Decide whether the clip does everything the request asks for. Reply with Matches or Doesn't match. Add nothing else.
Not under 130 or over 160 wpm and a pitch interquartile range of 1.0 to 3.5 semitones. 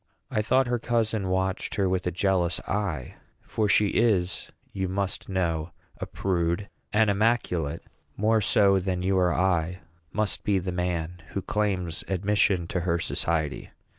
Matches